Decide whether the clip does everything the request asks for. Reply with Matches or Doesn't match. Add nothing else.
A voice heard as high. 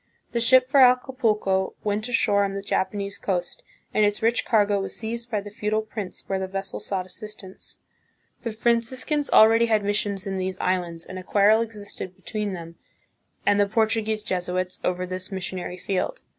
Matches